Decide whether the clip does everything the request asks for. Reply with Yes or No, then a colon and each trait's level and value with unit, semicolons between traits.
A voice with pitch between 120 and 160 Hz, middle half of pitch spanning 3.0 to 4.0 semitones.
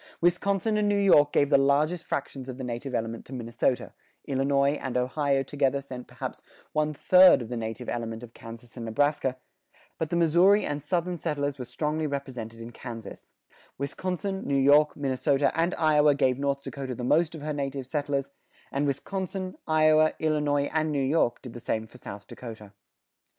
Yes: medium, 140 Hz; average, 3.6 semitones